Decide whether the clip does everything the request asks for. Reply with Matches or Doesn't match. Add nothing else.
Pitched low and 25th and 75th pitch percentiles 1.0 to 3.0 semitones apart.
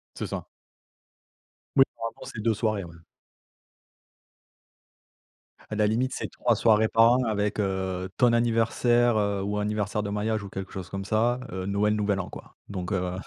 Matches